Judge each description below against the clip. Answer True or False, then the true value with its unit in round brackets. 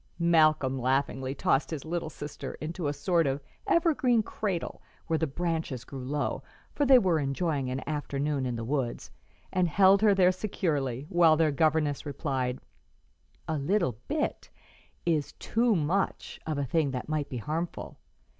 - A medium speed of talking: True (155 wpm)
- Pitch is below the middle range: False (155 Hz)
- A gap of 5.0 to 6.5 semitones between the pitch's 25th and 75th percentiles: False (4.2 semitones)